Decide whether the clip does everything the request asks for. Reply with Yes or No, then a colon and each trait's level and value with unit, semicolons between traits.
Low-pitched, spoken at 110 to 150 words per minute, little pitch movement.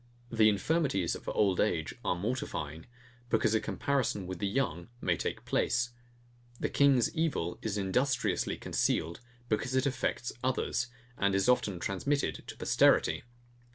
No: low, 110 Hz; average, 140 wpm; wide, 5.5 semitones